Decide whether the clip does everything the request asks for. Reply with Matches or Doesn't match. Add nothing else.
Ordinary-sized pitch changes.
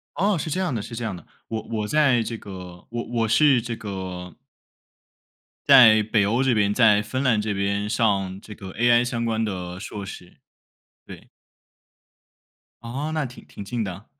Matches